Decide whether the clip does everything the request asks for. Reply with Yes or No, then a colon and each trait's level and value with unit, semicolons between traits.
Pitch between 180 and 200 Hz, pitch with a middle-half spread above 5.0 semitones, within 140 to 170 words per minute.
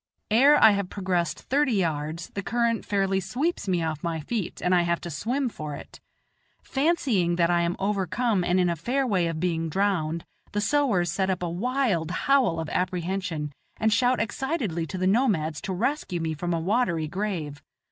No: medium, 185 Hz; wide, 5.4 semitones; average, 190 wpm